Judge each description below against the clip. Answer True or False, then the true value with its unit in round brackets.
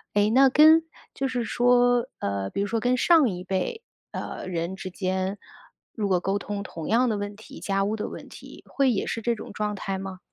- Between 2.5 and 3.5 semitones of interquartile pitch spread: False (4.4 semitones)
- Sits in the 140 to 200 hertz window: False (210 Hz)